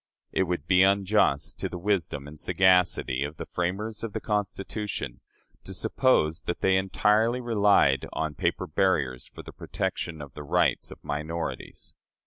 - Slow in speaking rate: No, average, 155 wpm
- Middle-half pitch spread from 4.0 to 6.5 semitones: Yes, average, 5.2 semitones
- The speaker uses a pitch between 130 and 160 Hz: No, very low, 90 Hz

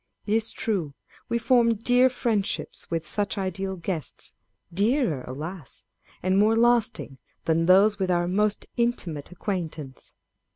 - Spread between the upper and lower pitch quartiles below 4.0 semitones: No, average, 5.1 semitones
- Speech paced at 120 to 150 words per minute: Yes, slow, 135 wpm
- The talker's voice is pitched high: Yes, high, 195 Hz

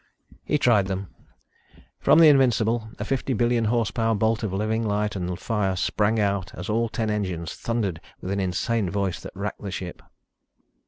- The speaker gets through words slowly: No, average, 170 wpm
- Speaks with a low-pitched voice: Yes, low, 105 Hz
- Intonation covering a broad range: No, average, 3.1 semitones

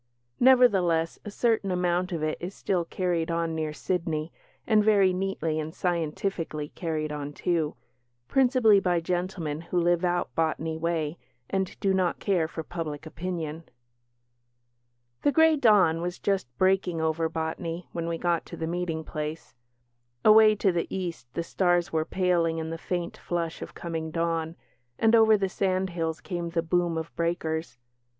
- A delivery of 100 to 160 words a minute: Yes, average, 155 wpm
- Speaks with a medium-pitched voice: Yes, medium, 170 Hz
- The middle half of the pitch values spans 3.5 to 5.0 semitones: No, narrow, 2.6 semitones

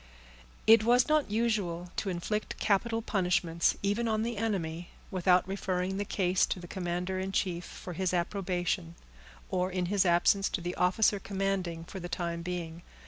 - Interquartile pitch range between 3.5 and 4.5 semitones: No, narrow, 2.5 semitones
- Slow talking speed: No, average, 165 wpm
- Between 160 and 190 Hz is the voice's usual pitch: Yes, medium, 185 Hz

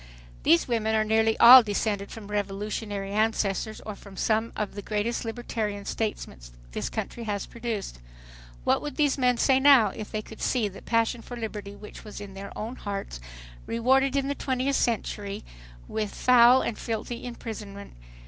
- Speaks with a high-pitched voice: Yes, high, 220 Hz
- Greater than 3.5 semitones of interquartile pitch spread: No, average, 2.7 semitones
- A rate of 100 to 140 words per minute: No, average, 165 wpm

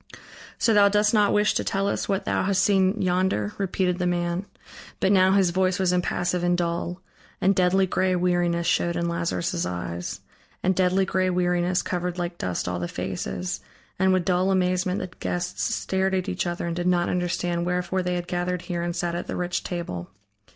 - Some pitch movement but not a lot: No, narrow, 1.5 semitones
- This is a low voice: No, medium, 180 Hz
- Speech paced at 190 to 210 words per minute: Yes, average, 195 wpm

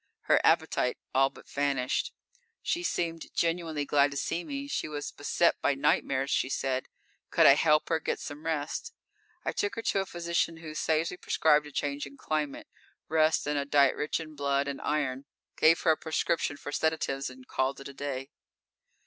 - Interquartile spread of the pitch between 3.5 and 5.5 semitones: No, narrow, 2.6 semitones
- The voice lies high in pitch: No, medium, 150 Hz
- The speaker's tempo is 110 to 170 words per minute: No, average, 185 wpm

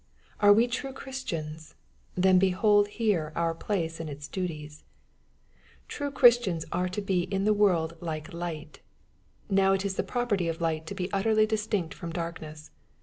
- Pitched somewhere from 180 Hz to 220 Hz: Yes, medium, 185 Hz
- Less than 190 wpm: Yes, average, 160 wpm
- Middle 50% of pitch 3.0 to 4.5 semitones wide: Yes, average, 4.1 semitones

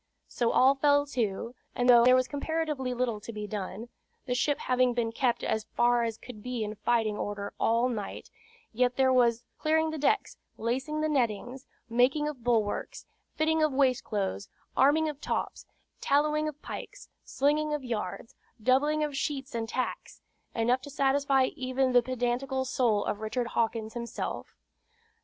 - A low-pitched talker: No, very high, 250 Hz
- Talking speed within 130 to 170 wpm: Yes, average, 165 wpm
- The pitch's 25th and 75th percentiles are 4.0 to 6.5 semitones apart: No, average, 3.5 semitones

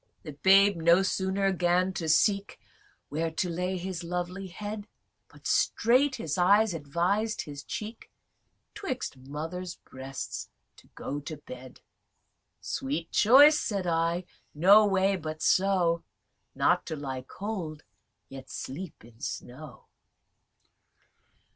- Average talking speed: No, slow, 120 wpm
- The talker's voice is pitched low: No, medium, 175 Hz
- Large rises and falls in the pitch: No, average, 4.2 semitones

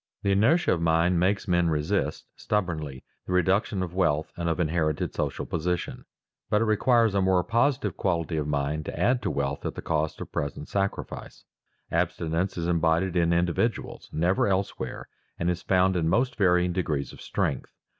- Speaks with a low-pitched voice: Yes, very low, 90 Hz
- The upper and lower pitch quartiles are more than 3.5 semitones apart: No, average, 3.2 semitones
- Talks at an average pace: Yes, average, 175 wpm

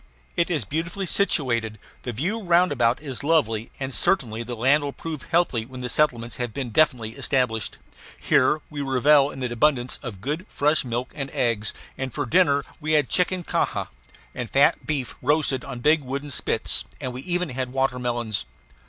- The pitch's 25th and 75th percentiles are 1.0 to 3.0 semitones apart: No, average, 3.9 semitones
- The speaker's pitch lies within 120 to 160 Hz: Yes, low, 135 Hz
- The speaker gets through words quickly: No, average, 170 wpm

